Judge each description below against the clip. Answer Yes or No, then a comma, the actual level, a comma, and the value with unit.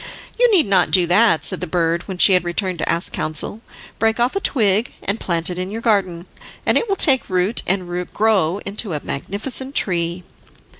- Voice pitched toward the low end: No, high, 190 Hz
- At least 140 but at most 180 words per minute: No, average, 200 wpm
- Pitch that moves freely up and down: No, average, 4.2 semitones